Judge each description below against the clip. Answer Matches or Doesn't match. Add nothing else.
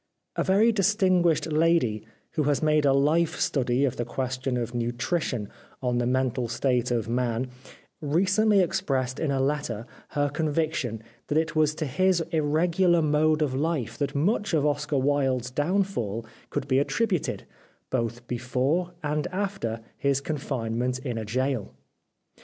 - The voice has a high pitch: Doesn't match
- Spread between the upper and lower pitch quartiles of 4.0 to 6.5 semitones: Matches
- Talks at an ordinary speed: Matches